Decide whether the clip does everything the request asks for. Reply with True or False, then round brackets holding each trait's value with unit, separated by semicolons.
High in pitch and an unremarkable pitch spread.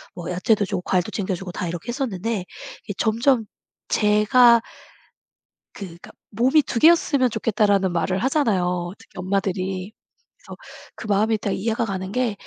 True (205 Hz; 3.8 semitones)